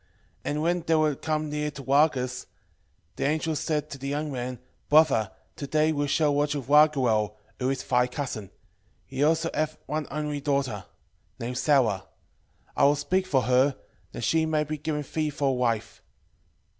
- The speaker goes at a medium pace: Yes, average, 180 wpm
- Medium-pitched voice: Yes, medium, 145 Hz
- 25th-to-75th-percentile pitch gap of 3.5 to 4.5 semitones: No, average, 3.1 semitones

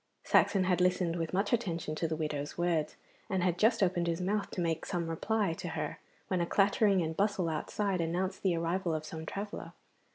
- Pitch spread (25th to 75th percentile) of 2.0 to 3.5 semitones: Yes, average, 3.0 semitones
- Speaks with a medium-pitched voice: Yes, medium, 175 Hz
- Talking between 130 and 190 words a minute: No, average, 200 wpm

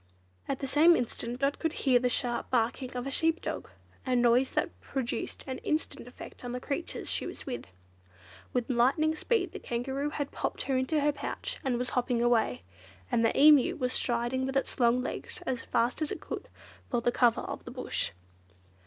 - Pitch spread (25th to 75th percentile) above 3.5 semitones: No, narrow, 2.5 semitones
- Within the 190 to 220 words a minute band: Yes, average, 195 wpm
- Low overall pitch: No, very high, 255 Hz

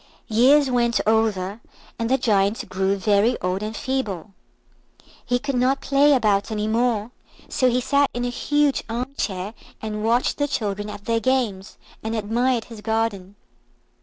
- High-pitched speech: Yes, high, 225 Hz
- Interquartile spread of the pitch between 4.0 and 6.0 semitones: No, average, 3.4 semitones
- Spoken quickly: No, average, 155 wpm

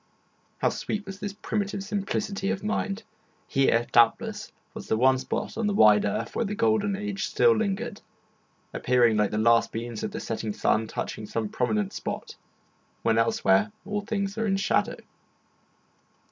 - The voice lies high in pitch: Yes, high, 195 Hz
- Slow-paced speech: No, average, 160 wpm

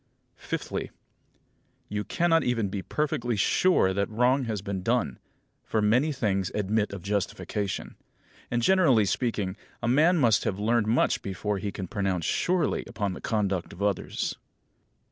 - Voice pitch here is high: No, low, 105 Hz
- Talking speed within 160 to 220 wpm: No, average, 145 wpm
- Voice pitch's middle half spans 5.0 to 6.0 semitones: No, average, 3.8 semitones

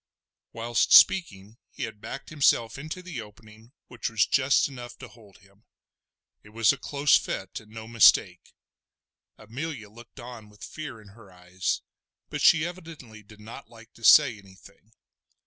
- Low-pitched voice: Yes, low, 115 Hz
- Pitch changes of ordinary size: Yes, average, 4.0 semitones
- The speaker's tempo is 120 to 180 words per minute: Yes, average, 160 wpm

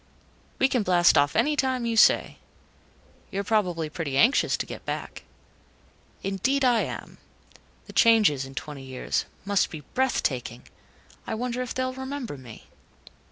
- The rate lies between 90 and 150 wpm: Yes, average, 140 wpm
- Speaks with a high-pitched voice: Yes, high, 210 Hz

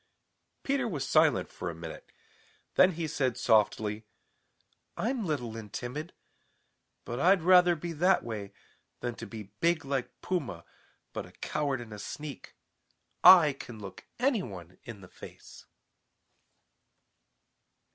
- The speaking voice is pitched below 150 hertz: Yes, low, 135 Hz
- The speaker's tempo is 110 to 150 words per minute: Yes, slow, 135 wpm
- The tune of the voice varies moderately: No, wide, 8.3 semitones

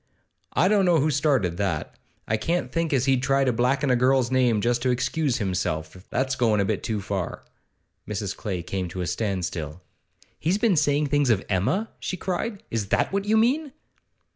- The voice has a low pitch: Yes, low, 125 Hz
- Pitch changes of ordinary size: No, wide, 7.4 semitones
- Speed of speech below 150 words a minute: No, average, 190 wpm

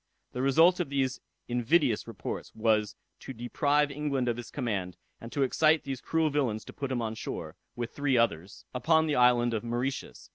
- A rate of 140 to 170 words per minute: No, average, 185 wpm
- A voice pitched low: Yes, low, 125 Hz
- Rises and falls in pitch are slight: No, average, 3.8 semitones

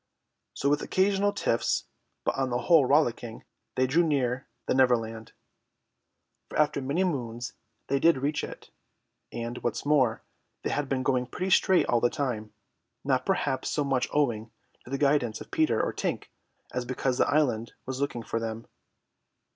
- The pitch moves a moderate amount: Yes, average, 3.5 semitones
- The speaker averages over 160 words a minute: Yes, average, 170 wpm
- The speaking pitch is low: Yes, low, 130 Hz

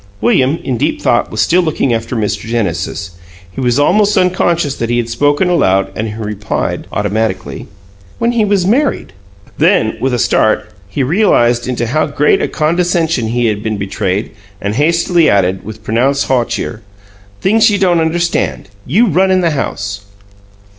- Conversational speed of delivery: Yes, average, 165 wpm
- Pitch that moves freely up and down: Yes, wide, 8.0 semitones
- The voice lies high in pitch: No, low, 130 Hz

